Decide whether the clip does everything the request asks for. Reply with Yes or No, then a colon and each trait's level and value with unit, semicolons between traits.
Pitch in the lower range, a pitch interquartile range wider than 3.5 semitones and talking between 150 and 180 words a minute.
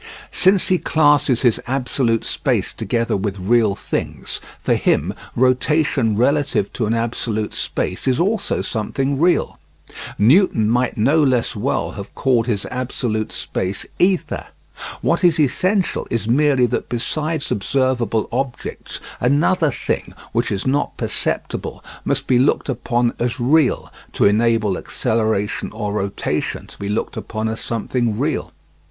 No: low, 125 Hz; average, 4.4 semitones; slow, 135 wpm